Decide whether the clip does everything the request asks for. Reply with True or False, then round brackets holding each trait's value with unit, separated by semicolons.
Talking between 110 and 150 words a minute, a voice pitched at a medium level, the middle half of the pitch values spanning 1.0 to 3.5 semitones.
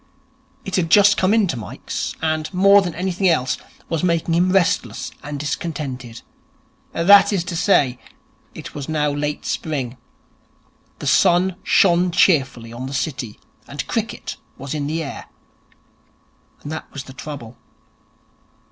False (140 wpm; 155 Hz; 4.8 semitones)